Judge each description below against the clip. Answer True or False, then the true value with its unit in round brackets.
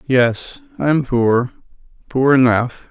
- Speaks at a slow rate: True (125 wpm)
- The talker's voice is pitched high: False (135 Hz)